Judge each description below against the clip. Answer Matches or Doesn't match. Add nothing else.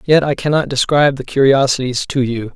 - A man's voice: Matches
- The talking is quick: Doesn't match